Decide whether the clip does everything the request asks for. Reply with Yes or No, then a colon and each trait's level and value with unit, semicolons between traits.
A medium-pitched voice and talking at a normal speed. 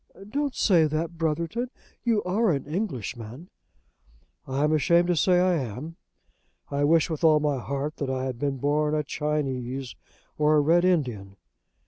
Yes: medium, 150 Hz; average, 160 wpm